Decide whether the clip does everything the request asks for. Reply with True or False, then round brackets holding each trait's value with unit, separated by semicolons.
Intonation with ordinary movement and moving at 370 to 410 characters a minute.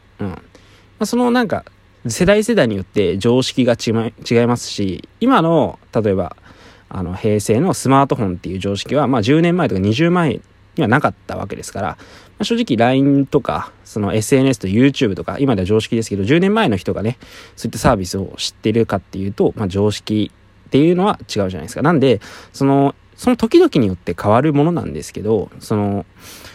False (6.0 semitones; 395 characters per minute)